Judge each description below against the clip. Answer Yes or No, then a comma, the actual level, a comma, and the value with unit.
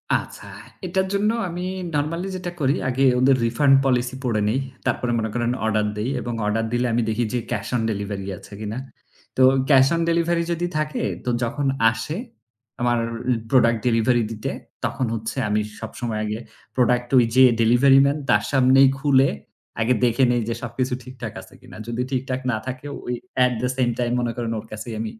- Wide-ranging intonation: No, average, 2.9 semitones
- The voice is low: Yes, low, 125 Hz